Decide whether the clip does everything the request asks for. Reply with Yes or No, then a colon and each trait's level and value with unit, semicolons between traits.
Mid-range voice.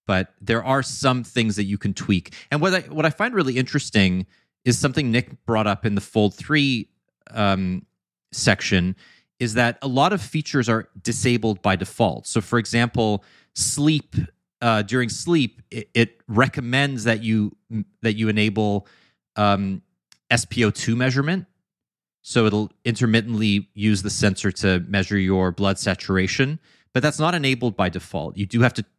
No: low, 115 Hz